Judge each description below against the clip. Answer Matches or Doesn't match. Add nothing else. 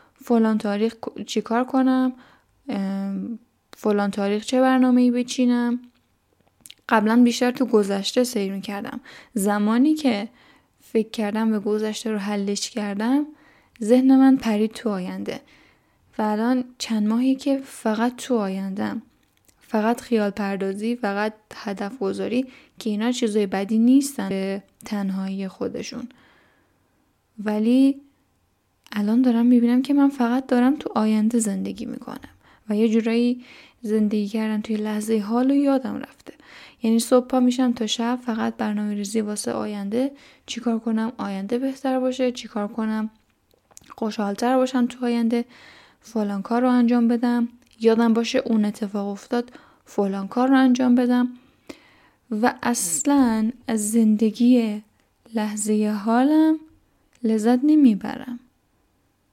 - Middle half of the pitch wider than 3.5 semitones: Doesn't match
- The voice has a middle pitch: Doesn't match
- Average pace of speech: Matches